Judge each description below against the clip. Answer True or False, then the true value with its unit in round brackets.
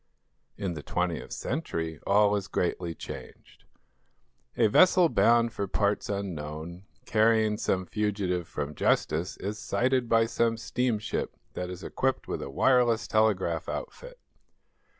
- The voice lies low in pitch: True (105 Hz)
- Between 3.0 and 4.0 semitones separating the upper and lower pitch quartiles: False (4.5 semitones)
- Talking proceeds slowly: True (130 wpm)